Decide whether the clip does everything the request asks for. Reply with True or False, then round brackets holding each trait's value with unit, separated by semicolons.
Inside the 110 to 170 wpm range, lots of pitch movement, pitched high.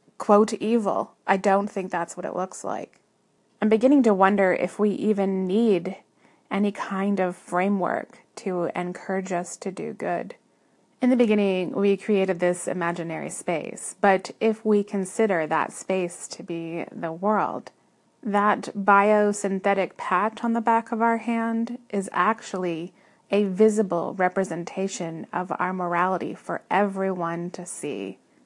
False (140 wpm; 3.0 semitones; 195 Hz)